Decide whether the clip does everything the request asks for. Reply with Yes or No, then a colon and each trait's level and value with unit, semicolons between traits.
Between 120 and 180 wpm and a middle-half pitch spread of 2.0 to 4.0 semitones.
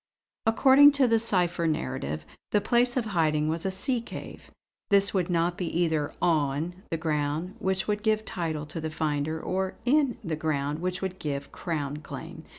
No: average, 175 wpm; average, 4.9 semitones